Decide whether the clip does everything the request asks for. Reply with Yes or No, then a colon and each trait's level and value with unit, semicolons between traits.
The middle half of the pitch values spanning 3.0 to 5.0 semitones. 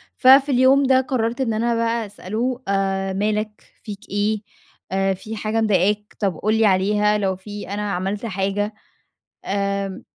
No: narrow, 2.5 semitones